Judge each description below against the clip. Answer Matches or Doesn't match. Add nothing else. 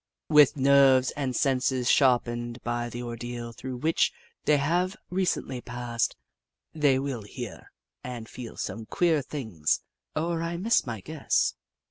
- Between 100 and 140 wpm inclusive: Matches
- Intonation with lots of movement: Doesn't match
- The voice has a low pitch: Matches